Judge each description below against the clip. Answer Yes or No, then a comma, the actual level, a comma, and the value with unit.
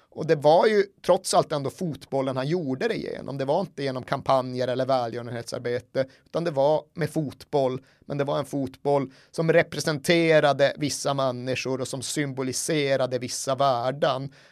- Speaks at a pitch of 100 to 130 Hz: No, medium, 140 Hz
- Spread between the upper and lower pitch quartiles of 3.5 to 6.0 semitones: No, average, 2.8 semitones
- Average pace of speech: Yes, average, 155 wpm